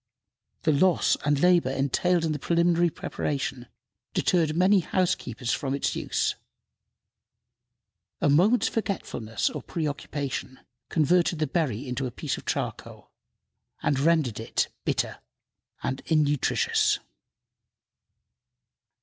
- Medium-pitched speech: Yes, medium, 150 Hz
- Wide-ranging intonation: No, average, 4.4 semitones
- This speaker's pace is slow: Yes, slow, 105 wpm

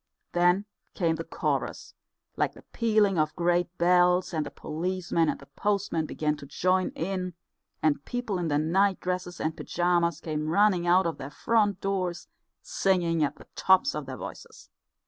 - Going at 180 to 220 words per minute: No, average, 165 wpm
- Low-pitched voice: No, medium, 175 Hz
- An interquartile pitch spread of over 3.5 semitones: No, average, 2.7 semitones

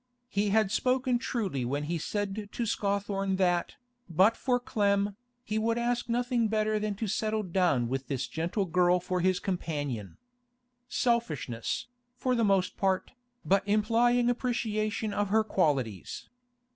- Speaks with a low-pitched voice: No, high, 205 Hz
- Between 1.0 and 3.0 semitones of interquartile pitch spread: No, average, 4.3 semitones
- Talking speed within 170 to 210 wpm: No, average, 145 wpm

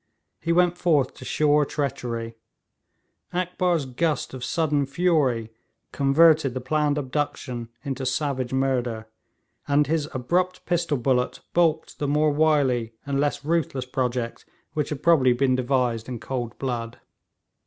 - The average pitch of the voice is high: No, medium, 140 Hz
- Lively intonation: No, average, 3.6 semitones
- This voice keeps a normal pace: No, slow, 130 wpm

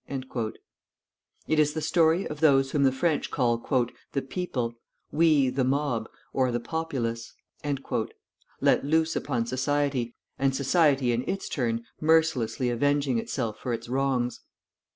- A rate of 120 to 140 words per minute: Yes, slow, 135 wpm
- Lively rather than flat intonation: No, average, 3.6 semitones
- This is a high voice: No, low, 135 Hz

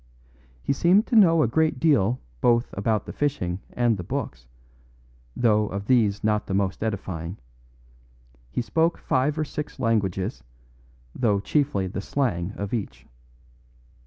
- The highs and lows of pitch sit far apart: Yes, wide, 6.1 semitones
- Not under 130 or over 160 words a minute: Yes, average, 140 wpm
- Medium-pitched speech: No, low, 110 Hz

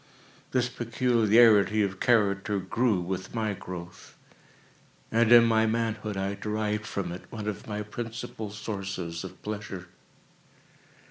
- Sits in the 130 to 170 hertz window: No, low, 105 Hz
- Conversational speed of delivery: No, slow, 125 wpm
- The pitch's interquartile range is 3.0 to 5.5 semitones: No, narrow, 2.6 semitones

